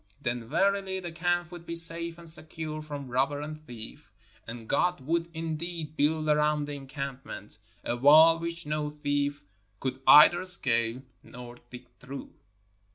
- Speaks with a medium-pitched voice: Yes, medium, 150 Hz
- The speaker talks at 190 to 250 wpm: No, average, 150 wpm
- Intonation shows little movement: No, average, 3.8 semitones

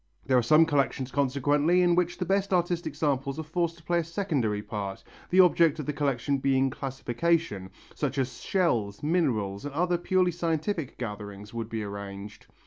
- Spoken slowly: No, average, 175 wpm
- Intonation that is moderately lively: No, wide, 6.2 semitones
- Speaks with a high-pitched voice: No, medium, 145 Hz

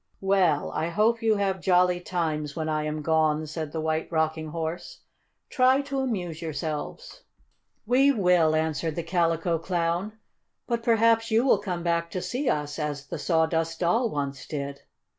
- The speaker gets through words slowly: No, average, 160 wpm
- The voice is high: No, medium, 170 Hz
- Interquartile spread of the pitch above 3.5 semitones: Yes, average, 4.3 semitones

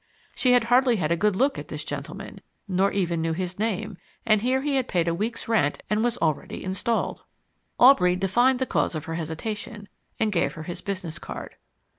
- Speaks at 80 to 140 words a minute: No, average, 200 wpm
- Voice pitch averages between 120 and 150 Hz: No, high, 200 Hz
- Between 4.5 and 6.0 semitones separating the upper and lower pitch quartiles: Yes, wide, 5.5 semitones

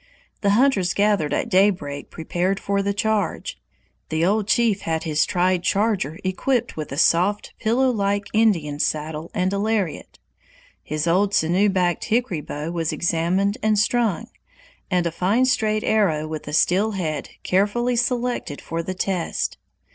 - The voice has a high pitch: Yes, high, 195 Hz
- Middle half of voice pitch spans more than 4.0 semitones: Yes, average, 4.4 semitones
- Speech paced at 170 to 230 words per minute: No, average, 155 wpm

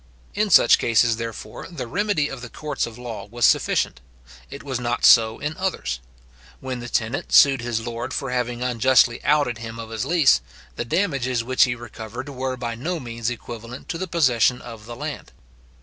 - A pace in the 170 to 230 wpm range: Yes, average, 185 wpm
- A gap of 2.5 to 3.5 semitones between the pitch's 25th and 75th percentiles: Yes, average, 3.1 semitones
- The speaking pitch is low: Yes, low, 120 Hz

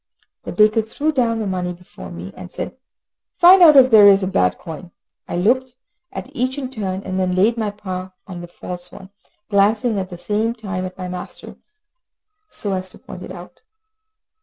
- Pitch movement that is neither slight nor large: Yes, average, 3.9 semitones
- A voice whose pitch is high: Yes, high, 195 Hz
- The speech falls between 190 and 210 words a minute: Yes, average, 195 wpm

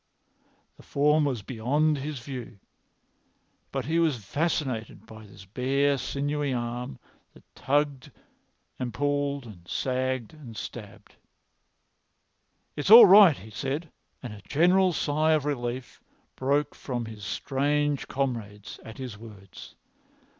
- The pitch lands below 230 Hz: Yes, low, 135 Hz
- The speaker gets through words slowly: Yes, slow, 125 wpm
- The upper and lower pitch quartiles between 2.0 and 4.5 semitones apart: Yes, average, 4.2 semitones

